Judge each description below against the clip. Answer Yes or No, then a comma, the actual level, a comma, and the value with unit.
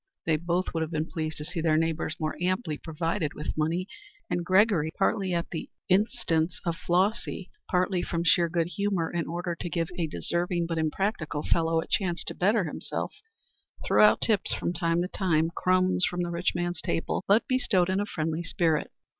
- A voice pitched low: No, medium, 170 Hz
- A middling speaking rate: Yes, average, 190 wpm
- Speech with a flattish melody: Yes, narrow, 2.2 semitones